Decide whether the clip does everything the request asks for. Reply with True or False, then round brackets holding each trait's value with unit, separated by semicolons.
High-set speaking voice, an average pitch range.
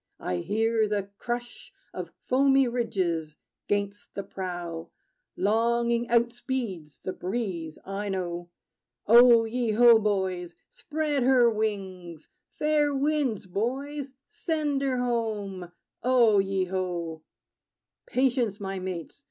True (220 Hz; 4.8 semitones)